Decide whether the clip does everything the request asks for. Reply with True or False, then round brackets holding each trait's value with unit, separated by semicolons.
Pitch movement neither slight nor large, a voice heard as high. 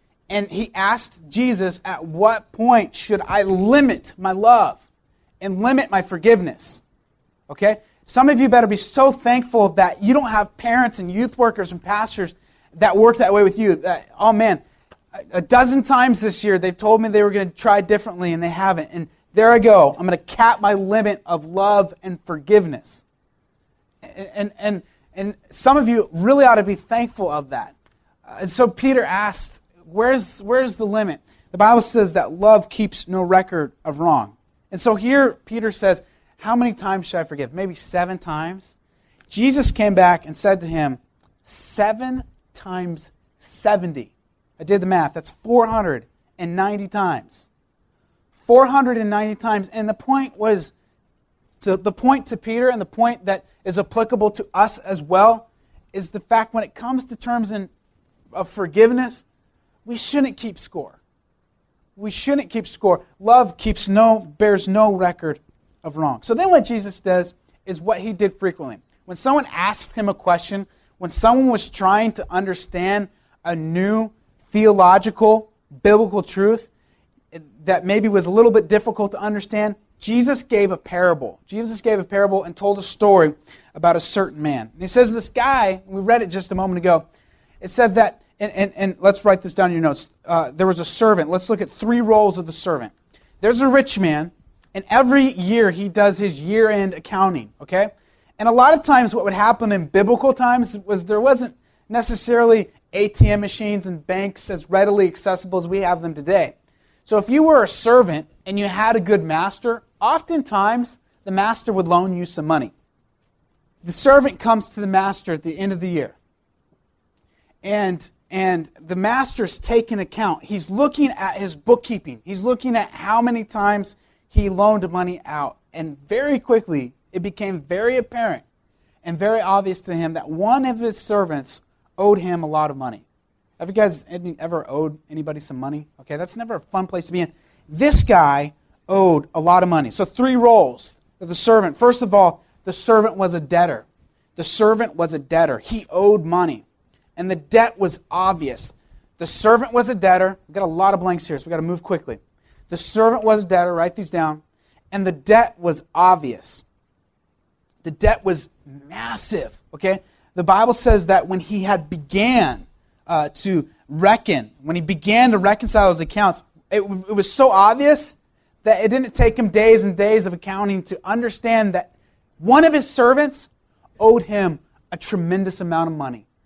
True (4.0 semitones; 200 Hz)